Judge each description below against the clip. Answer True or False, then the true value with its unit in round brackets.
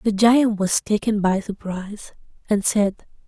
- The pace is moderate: True (145 wpm)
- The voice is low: False (205 Hz)